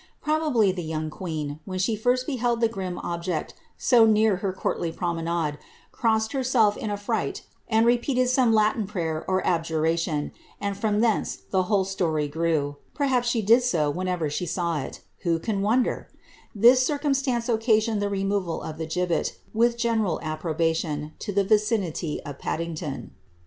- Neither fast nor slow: Yes, average, 165 wpm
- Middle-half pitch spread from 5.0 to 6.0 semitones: Yes, wide, 5.6 semitones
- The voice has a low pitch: No, high, 195 Hz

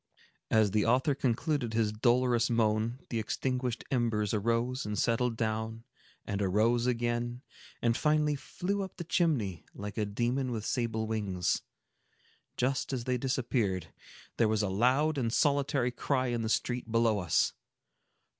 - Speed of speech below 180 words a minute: Yes, average, 145 wpm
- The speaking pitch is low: Yes, low, 120 Hz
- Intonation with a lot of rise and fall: No, average, 2.7 semitones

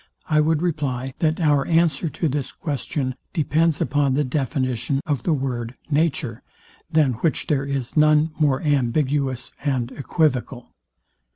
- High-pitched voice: No, medium, 145 Hz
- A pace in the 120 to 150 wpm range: Yes, slow, 135 wpm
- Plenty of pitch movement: No, average, 2.9 semitones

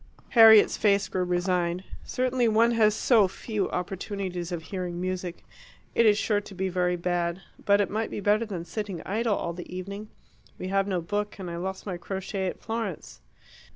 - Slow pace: No, average, 185 wpm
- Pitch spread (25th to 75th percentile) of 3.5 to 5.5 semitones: No, average, 2.9 semitones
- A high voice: Yes, high, 195 Hz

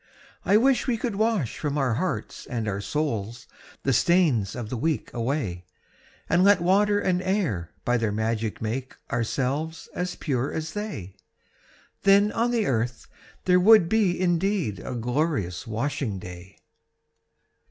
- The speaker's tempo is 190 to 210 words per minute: No, average, 145 wpm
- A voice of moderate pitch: Yes, medium, 145 Hz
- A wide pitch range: Yes, wide, 8.8 semitones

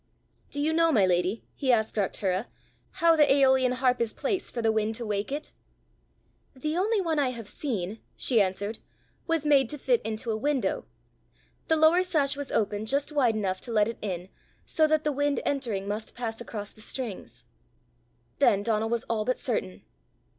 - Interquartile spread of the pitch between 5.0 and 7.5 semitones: Yes, average, 5.3 semitones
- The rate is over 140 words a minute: Yes, average, 185 wpm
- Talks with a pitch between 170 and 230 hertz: No, high, 240 Hz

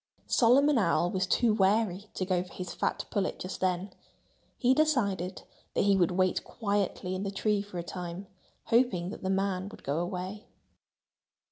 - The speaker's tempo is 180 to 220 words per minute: No, average, 170 wpm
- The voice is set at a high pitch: Yes, high, 195 Hz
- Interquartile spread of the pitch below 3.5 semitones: Yes, narrow, 2.6 semitones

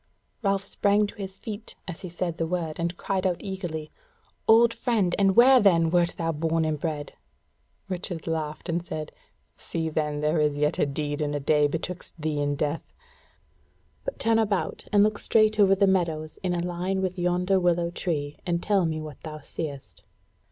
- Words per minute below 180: No, average, 185 wpm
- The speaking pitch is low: No, medium, 170 Hz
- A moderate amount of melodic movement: Yes, average, 3.8 semitones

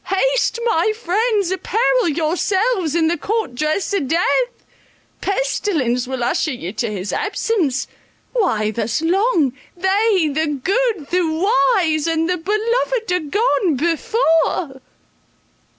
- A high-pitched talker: Yes, very high, 345 Hz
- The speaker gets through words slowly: Yes, slow, 120 wpm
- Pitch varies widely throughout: Yes, wide, 6.1 semitones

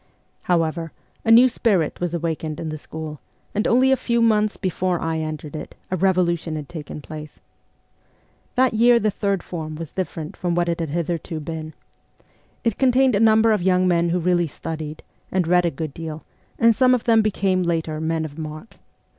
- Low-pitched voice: No, medium, 175 Hz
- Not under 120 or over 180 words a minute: No, average, 190 wpm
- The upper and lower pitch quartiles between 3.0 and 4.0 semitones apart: No, average, 4.6 semitones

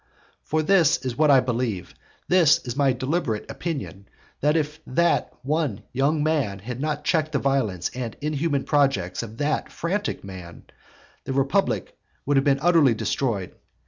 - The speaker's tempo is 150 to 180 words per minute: Yes, average, 155 wpm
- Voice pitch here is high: No, medium, 140 Hz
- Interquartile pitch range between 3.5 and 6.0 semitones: Yes, average, 4.5 semitones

